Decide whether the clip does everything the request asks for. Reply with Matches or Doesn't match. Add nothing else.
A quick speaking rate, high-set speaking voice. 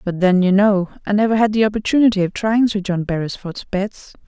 Matches